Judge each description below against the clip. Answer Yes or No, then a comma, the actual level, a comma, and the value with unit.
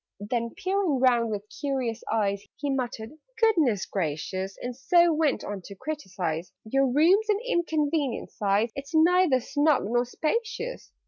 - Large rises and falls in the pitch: Yes, wide, 6.6 semitones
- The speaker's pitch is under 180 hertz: No, very high, 265 Hz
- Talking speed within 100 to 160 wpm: Yes, average, 140 wpm